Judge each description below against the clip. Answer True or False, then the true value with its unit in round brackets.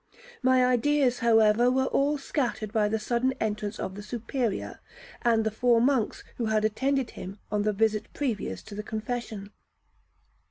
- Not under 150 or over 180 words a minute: True (160 wpm)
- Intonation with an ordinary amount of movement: True (3.1 semitones)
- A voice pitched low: False (225 Hz)